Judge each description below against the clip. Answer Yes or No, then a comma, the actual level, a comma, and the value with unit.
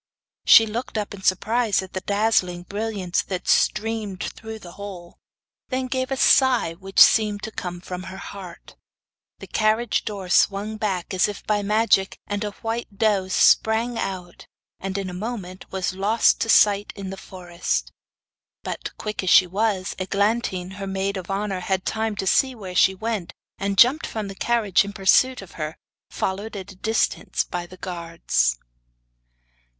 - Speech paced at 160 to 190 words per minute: Yes, average, 170 wpm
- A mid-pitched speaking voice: No, high, 200 Hz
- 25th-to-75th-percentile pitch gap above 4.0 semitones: No, average, 2.8 semitones